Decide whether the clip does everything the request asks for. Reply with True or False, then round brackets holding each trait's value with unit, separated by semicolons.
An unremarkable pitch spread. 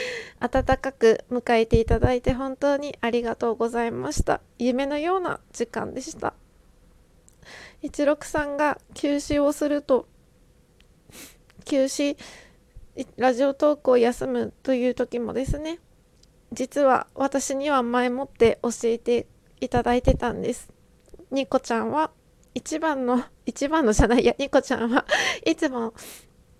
True (3.1 semitones)